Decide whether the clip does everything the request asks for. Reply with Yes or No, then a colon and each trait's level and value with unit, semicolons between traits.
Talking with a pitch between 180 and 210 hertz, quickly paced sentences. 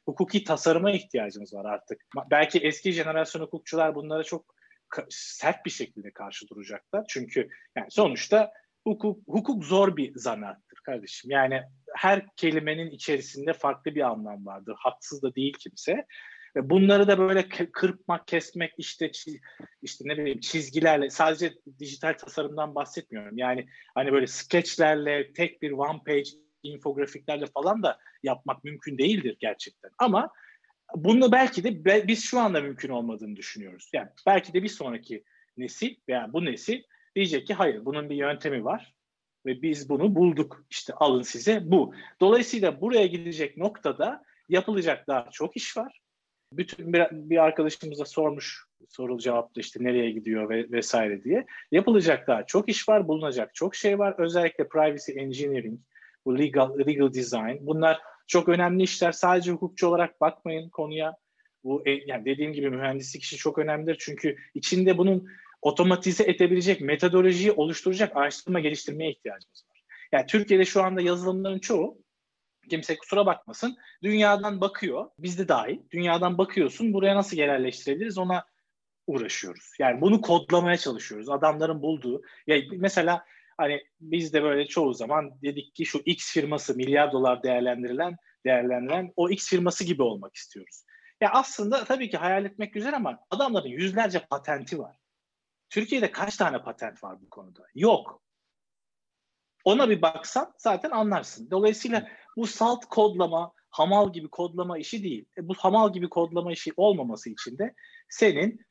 No: medium, 170 Hz; fast, 145 wpm